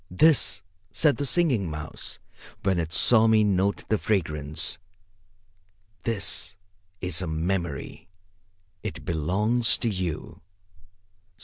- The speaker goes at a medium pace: No, slow, 105 wpm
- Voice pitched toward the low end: Yes, very low, 95 Hz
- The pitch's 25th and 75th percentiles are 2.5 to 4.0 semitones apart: No, average, 5.1 semitones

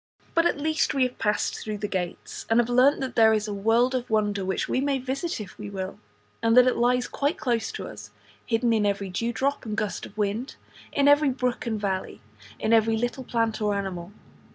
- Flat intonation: No, average, 3.6 semitones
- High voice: Yes, high, 225 Hz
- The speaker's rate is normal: No, fast, 220 wpm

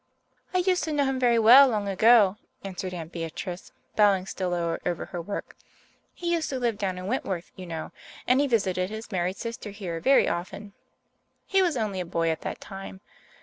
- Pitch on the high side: Yes, high, 200 Hz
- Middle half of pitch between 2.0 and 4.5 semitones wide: No, average, 5.2 semitones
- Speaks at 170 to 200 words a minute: Yes, average, 195 wpm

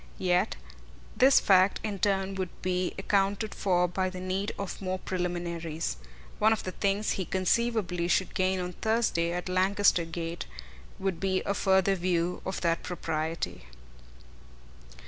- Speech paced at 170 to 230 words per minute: No, average, 145 wpm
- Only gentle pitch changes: Yes, narrow, 1.9 semitones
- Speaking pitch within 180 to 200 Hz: Yes, medium, 185 Hz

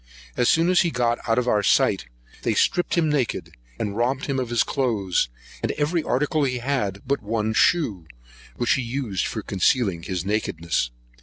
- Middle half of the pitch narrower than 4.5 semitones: No, wide, 5.4 semitones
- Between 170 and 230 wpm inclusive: Yes, average, 180 wpm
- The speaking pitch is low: Yes, low, 120 Hz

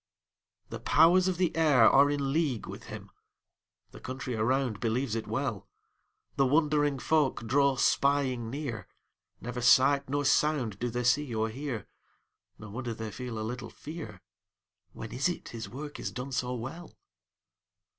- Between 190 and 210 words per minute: No, average, 155 wpm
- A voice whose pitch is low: Yes, low, 130 Hz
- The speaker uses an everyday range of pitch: Yes, average, 3.9 semitones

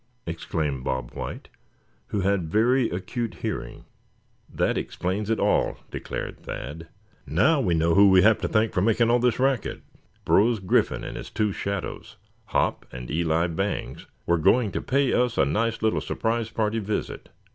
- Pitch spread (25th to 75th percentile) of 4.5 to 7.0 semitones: Yes, average, 5.0 semitones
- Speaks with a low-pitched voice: Yes, low, 105 Hz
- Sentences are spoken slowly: No, average, 165 wpm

